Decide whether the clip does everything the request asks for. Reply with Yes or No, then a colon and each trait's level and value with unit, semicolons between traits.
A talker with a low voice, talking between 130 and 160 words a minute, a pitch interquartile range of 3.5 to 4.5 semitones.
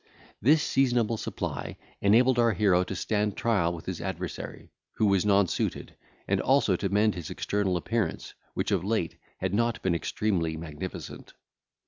Yes: low, 100 Hz; average, 150 wpm; average, 3.9 semitones